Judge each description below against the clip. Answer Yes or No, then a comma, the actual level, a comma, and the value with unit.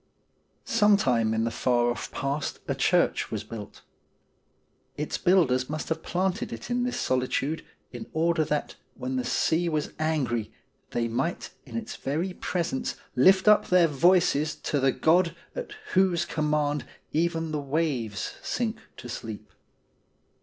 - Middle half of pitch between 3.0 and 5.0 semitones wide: No, wide, 5.6 semitones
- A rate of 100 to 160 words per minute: Yes, average, 140 wpm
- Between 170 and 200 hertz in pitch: No, medium, 155 Hz